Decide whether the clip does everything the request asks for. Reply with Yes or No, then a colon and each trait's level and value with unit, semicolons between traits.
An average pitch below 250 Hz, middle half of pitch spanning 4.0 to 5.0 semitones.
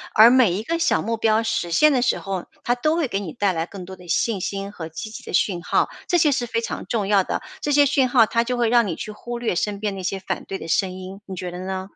Yes: high, 210 Hz; average, 4.3 semitones